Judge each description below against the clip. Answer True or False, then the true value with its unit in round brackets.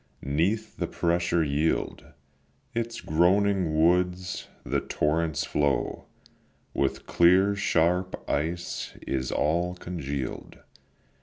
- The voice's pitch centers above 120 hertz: False (85 Hz)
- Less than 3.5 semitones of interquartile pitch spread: True (2.9 semitones)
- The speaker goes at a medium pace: False (90 wpm)